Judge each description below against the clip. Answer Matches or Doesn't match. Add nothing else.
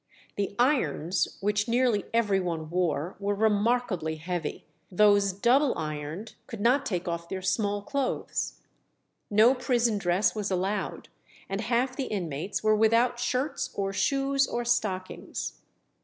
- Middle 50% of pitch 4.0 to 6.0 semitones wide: Matches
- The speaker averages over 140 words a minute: Doesn't match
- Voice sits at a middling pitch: Doesn't match